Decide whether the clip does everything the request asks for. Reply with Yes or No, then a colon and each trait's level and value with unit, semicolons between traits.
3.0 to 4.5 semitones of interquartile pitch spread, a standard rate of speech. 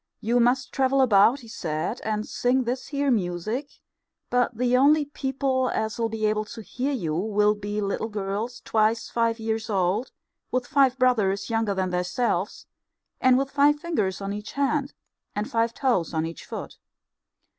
Yes: average, 4.0 semitones; average, 165 wpm